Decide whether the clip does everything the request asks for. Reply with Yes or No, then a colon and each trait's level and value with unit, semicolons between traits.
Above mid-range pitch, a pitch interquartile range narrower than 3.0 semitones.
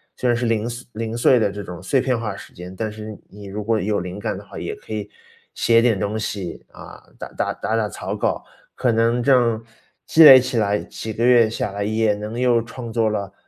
No: low, 110 Hz; narrow, 2.4 semitones